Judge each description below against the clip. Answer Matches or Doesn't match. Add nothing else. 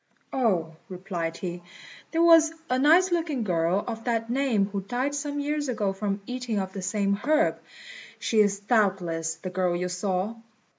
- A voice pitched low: Doesn't match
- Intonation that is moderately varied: Doesn't match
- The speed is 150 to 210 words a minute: Matches